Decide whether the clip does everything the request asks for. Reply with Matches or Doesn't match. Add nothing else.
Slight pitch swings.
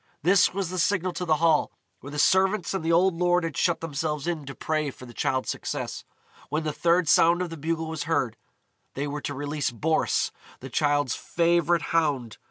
Doesn't match